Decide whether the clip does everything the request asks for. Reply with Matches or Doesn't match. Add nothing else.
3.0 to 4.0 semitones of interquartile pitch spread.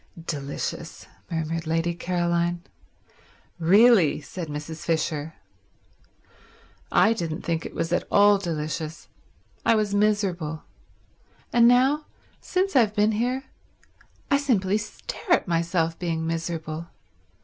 Doesn't match